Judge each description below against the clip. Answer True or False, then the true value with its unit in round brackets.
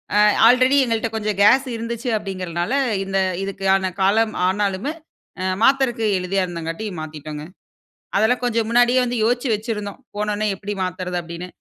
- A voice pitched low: False (210 Hz)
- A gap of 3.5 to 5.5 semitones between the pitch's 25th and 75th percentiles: True (4.0 semitones)